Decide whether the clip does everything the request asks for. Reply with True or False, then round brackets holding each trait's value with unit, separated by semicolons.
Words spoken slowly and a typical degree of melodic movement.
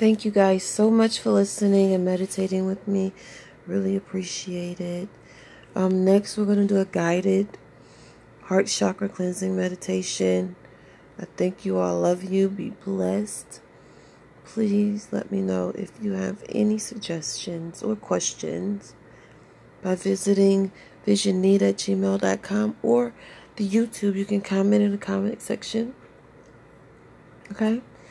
False (125 wpm; 2.1 semitones)